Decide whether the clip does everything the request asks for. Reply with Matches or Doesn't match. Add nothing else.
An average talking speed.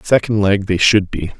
Matches